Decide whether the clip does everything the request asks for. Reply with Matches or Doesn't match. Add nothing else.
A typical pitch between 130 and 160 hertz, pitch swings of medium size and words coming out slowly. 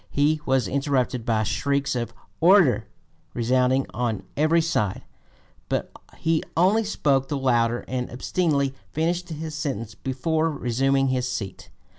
Matches